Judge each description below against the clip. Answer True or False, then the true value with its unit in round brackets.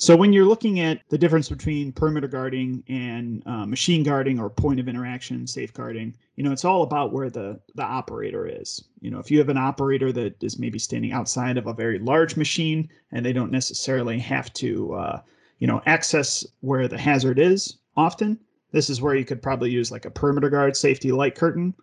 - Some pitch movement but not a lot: True (4.1 semitones)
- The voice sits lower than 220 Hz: True (140 Hz)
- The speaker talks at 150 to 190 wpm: False (205 wpm)